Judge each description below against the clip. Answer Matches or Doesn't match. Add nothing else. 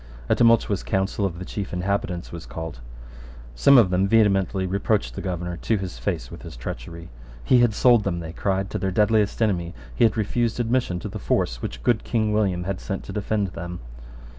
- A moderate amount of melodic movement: Matches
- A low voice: Matches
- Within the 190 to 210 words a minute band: Matches